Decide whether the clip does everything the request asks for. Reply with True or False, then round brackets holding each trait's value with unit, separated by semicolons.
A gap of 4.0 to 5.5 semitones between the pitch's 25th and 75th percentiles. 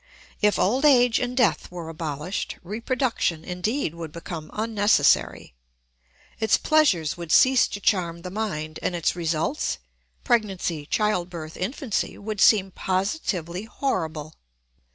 True (5.1 semitones)